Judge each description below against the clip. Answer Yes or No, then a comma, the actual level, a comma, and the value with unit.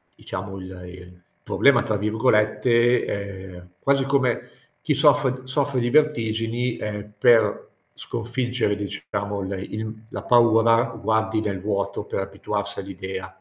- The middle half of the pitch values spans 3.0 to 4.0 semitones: Yes, average, 3.3 semitones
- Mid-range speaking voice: No, low, 110 Hz